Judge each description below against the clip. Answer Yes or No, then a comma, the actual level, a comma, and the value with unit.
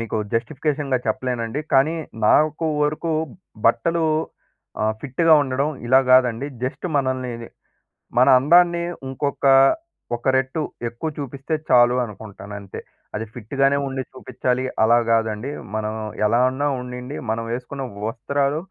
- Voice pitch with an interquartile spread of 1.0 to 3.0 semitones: No, average, 3.4 semitones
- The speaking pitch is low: Yes, low, 130 Hz